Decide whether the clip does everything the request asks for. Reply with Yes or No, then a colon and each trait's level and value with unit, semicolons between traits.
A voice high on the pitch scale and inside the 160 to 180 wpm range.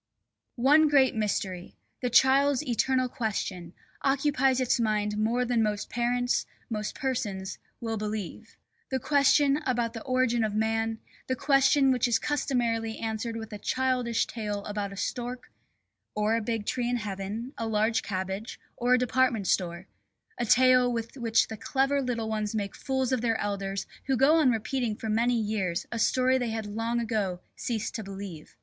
Yes: high, 230 Hz; average, 170 wpm